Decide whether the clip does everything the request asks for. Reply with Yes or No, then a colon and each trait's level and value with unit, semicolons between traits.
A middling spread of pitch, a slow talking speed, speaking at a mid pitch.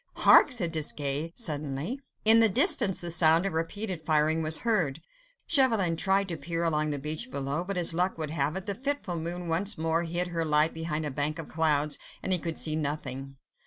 No: average, 3.4 semitones; average, 200 wpm; medium, 165 Hz